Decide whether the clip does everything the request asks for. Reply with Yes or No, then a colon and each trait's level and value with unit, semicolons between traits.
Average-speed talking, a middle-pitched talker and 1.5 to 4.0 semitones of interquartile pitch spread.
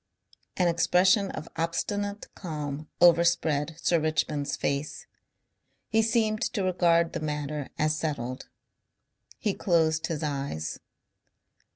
No: slow, 105 wpm; medium, 160 Hz; average, 3.5 semitones